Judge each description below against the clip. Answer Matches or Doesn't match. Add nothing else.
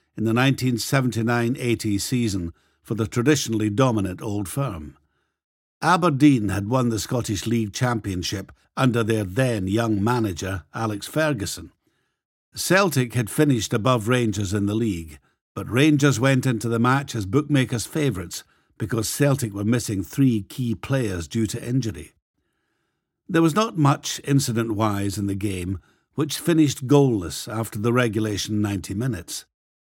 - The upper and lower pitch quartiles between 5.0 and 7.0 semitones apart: Doesn't match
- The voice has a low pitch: Matches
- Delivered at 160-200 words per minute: Doesn't match